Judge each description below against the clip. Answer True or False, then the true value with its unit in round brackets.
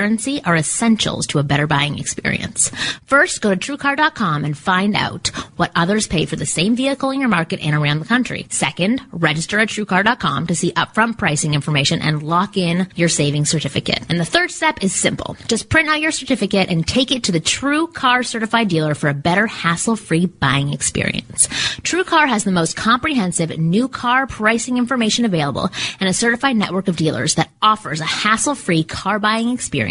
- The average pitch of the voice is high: True (195 Hz)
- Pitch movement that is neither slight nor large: False (6.7 semitones)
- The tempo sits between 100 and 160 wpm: False (185 wpm)